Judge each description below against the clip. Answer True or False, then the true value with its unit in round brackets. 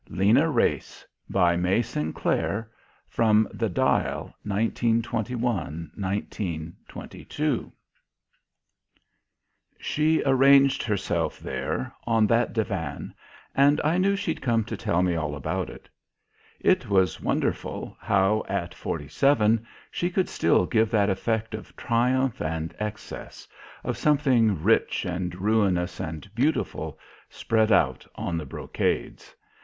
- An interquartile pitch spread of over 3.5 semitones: True (5.1 semitones)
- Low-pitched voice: True (110 Hz)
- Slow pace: True (115 wpm)